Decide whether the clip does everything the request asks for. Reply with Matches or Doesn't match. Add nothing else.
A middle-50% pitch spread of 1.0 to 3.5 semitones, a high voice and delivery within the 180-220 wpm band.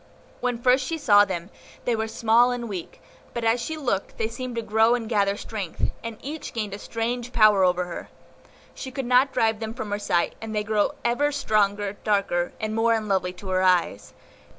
Matches